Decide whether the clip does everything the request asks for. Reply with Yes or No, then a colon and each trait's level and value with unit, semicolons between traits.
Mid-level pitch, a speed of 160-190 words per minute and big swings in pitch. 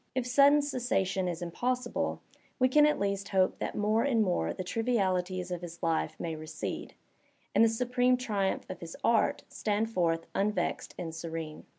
No: high, 200 Hz; average, 175 wpm; wide, 5.9 semitones